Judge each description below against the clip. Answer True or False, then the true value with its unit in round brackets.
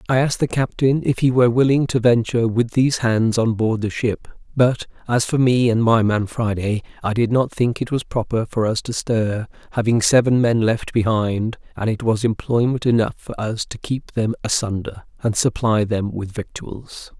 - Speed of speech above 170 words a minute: True (200 wpm)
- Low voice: True (115 Hz)